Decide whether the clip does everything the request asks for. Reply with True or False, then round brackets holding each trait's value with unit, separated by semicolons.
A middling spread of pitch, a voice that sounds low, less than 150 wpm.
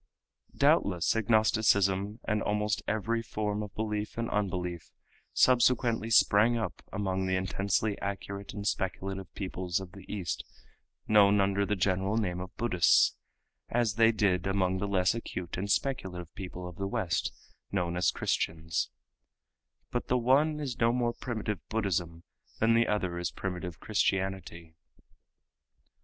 True (3.0 semitones; 100 Hz; 140 wpm)